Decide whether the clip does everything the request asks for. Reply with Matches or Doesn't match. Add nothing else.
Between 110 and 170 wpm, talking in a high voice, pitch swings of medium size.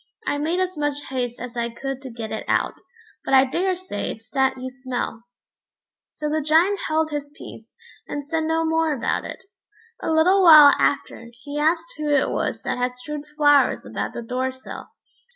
Doesn't match